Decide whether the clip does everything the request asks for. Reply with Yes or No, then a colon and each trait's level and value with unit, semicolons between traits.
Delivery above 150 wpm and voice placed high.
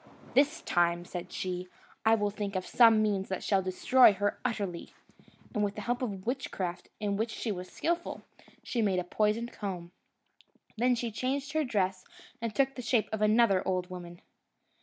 Yes: average, 180 wpm; high, 210 Hz